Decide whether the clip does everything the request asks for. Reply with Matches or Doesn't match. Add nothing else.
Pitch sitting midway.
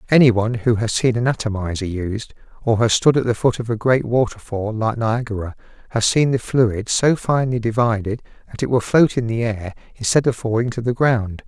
Doesn't match